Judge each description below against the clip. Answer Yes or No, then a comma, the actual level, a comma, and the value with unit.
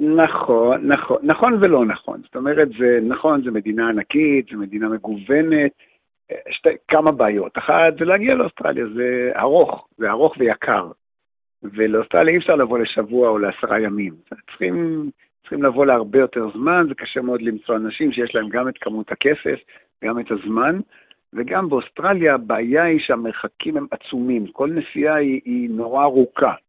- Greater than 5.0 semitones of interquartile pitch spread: Yes, wide, 5.5 semitones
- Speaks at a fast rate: Yes, fast, 155 wpm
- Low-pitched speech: Yes, low, 130 Hz